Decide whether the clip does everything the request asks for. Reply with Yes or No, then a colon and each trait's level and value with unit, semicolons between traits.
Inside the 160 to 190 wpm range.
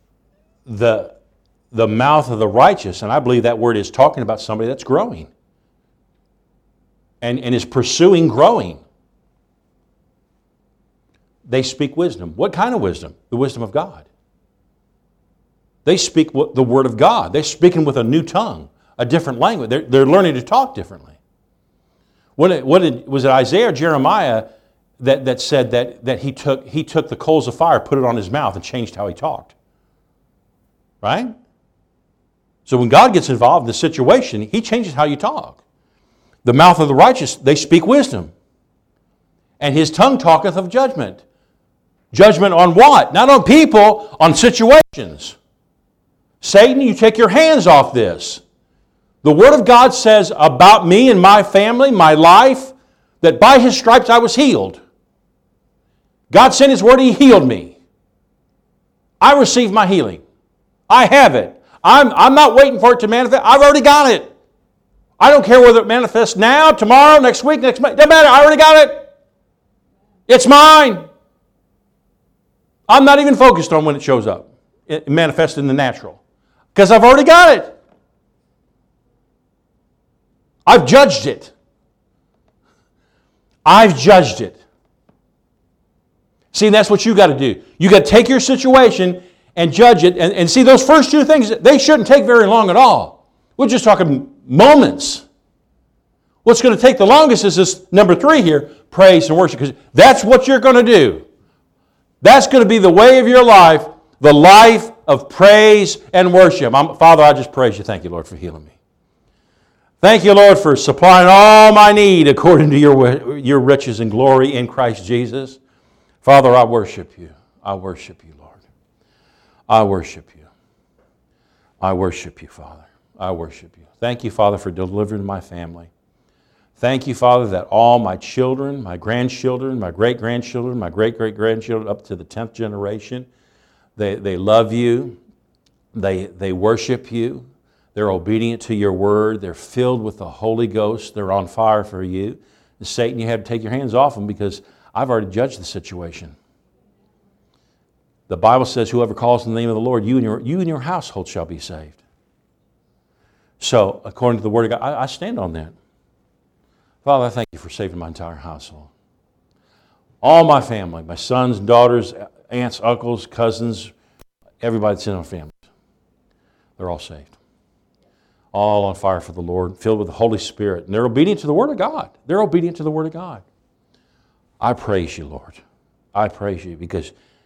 Yes: average, 170 wpm